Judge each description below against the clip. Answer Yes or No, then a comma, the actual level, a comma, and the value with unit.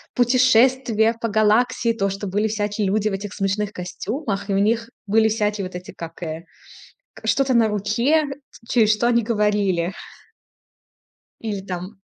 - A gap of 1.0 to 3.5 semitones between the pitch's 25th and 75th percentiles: Yes, average, 2.7 semitones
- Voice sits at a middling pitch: No, high, 210 Hz